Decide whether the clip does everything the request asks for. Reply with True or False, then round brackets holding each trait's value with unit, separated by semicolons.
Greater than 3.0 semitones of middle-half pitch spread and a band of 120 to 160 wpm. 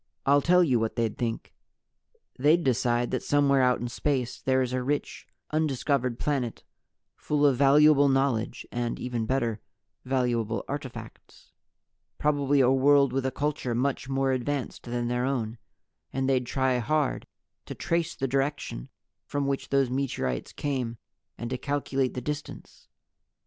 False (2.7 semitones; 150 wpm)